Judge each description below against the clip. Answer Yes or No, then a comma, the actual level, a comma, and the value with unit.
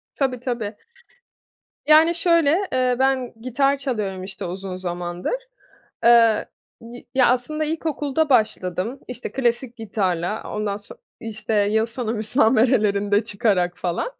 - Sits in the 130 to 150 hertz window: No, high, 230 Hz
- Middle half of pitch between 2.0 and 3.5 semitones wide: No, average, 4.4 semitones